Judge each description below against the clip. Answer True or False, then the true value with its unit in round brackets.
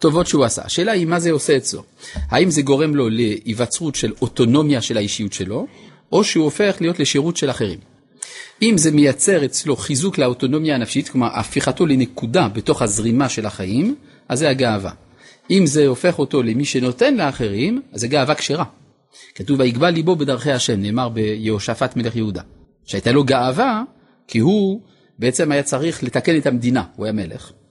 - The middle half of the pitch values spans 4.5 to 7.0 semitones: True (5.1 semitones)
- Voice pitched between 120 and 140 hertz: True (135 Hz)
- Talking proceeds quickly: True (165 wpm)